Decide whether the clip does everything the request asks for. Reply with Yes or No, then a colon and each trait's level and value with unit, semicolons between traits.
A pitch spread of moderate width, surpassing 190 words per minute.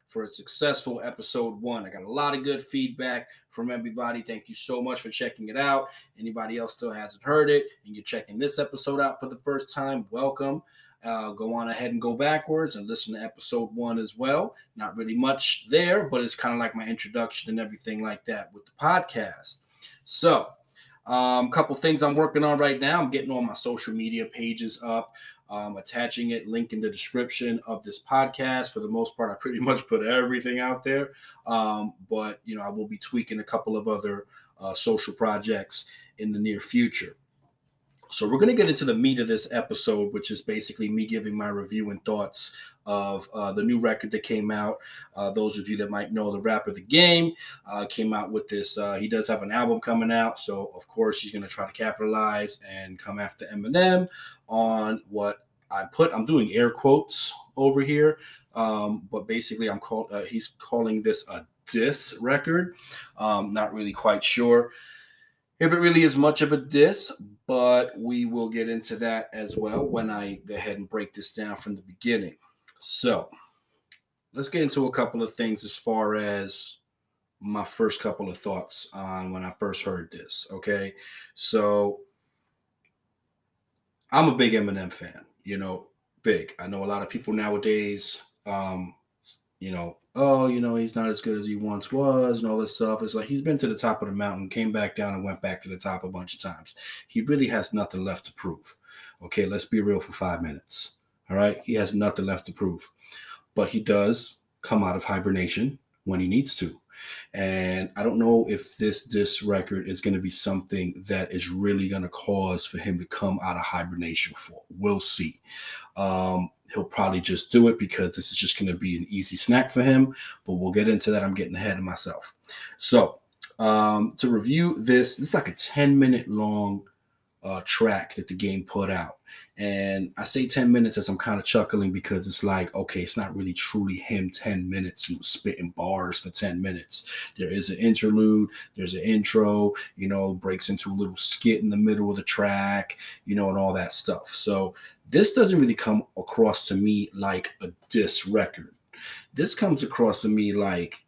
Yes: average, 4.6 semitones; average, 200 wpm